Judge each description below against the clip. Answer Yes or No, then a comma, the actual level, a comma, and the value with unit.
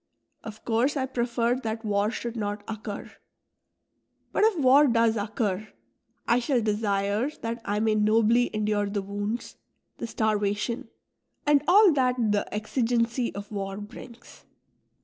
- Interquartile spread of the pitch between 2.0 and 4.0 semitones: Yes, average, 2.7 semitones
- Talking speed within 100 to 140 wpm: Yes, slow, 135 wpm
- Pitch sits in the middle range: No, high, 225 Hz